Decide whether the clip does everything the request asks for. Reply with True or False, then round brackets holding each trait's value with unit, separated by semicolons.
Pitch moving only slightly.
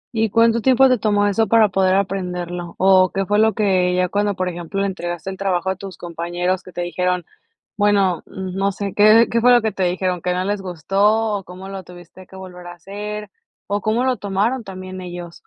True (2.3 semitones)